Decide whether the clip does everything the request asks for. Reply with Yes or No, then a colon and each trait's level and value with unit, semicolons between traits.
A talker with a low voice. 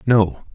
Yes: low, 110 Hz